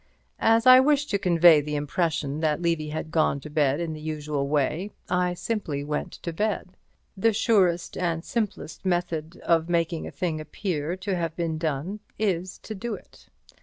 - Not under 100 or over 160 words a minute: No, average, 175 wpm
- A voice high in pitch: No, medium, 170 Hz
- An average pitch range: Yes, average, 3.6 semitones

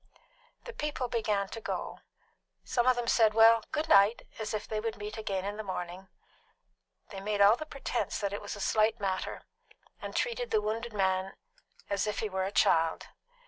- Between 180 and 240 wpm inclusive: Yes, average, 190 wpm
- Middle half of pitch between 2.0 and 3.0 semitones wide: Yes, narrow, 2.5 semitones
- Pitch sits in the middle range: No, high, 215 Hz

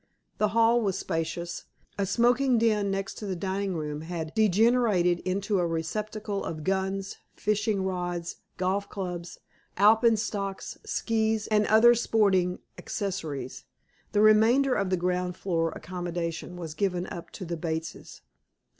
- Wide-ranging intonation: No, average, 3.5 semitones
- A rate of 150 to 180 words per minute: No, slow, 135 wpm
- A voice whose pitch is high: Yes, high, 195 Hz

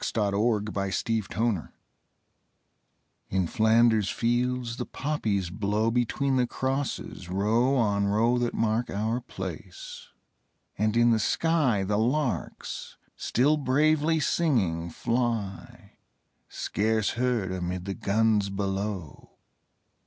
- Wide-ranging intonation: No, average, 3.7 semitones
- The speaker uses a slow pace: Yes, slow, 110 wpm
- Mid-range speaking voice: No, low, 110 Hz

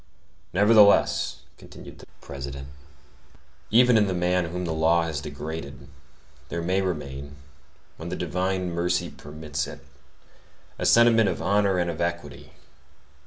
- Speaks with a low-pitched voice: Yes, very low, 85 Hz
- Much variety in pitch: No, average, 3.4 semitones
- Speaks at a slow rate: Yes, slow, 130 wpm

